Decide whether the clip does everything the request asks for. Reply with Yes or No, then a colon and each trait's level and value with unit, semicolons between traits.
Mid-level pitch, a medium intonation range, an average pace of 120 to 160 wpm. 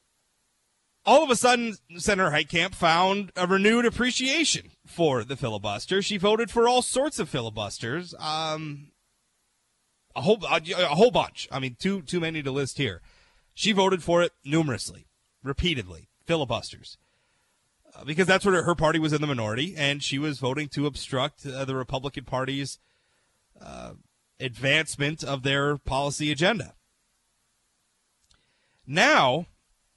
No: medium, 155 Hz; wide, 5.7 semitones; average, 140 wpm